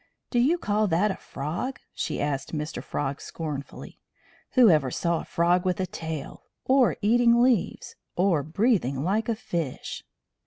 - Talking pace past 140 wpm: Yes, average, 150 wpm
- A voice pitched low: No, medium, 180 Hz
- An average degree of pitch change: No, wide, 6.7 semitones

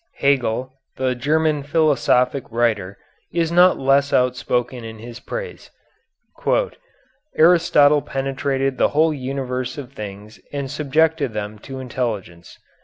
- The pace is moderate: No, slow, 110 wpm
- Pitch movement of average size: Yes, average, 3.3 semitones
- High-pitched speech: No, low, 135 Hz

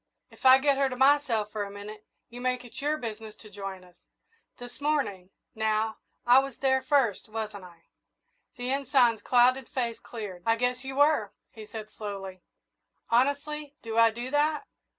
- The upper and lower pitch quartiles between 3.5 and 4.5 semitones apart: Yes, average, 4.0 semitones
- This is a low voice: No, high, 240 Hz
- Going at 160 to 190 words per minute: Yes, average, 170 wpm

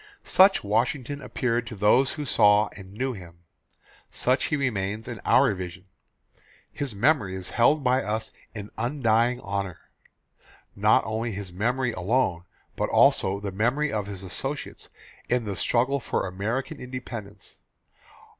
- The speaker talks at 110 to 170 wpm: Yes, average, 140 wpm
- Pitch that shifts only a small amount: No, average, 4.3 semitones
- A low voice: Yes, low, 110 Hz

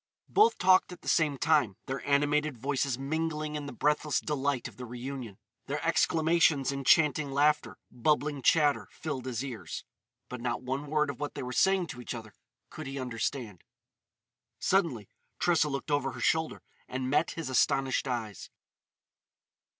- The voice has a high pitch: No, medium, 140 Hz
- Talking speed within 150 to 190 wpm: Yes, average, 160 wpm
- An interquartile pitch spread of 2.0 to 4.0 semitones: Yes, average, 3.1 semitones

